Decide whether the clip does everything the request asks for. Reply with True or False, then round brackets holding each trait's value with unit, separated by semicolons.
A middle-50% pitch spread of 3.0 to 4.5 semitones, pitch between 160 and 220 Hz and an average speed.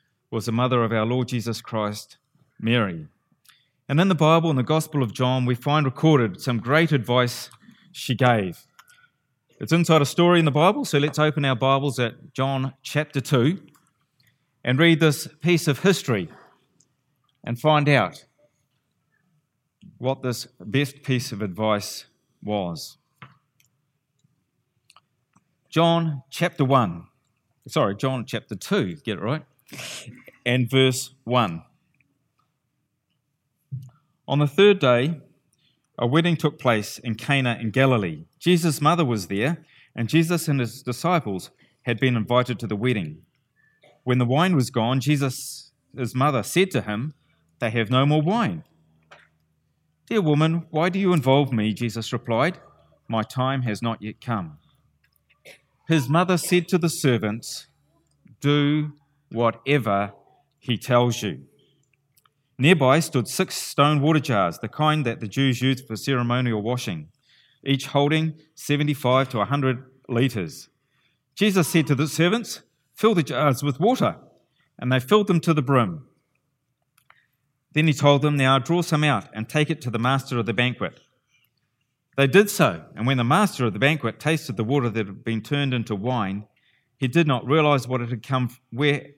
False (3.9 semitones; 135 Hz; 150 wpm)